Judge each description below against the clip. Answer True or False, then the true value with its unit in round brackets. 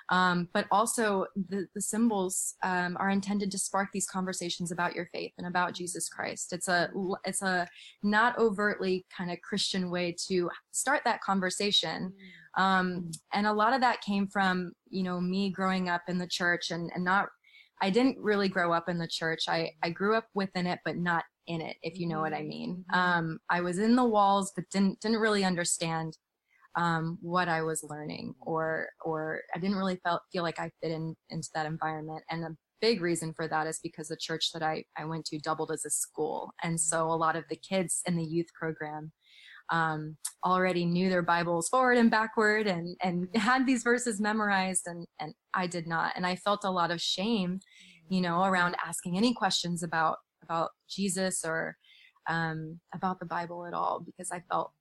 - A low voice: False (180 Hz)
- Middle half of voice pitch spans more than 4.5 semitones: False (2.9 semitones)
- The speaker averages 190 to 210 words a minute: True (200 wpm)